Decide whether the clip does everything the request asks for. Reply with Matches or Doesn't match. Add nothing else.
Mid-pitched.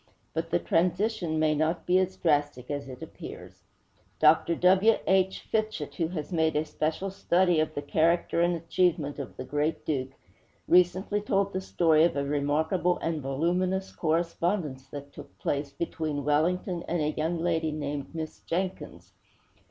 Matches